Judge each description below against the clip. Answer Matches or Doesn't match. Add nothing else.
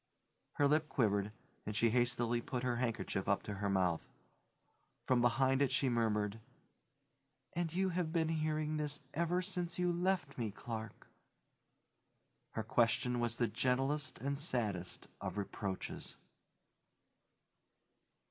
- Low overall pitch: Matches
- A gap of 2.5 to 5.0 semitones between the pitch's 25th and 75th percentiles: Doesn't match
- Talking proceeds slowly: Matches